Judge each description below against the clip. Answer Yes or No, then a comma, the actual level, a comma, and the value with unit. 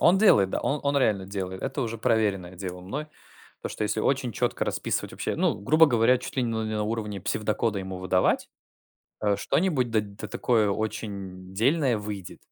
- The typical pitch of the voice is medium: No, low, 110 Hz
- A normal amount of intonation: Yes, average, 4.3 semitones